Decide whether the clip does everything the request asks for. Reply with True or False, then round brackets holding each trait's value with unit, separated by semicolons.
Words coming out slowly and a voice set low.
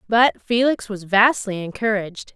False (125 wpm; 215 Hz)